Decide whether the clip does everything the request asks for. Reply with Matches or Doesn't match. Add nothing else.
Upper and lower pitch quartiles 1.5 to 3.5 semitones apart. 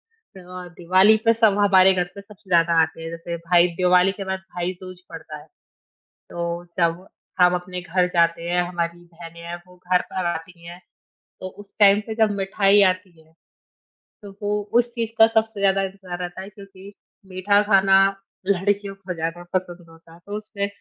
Matches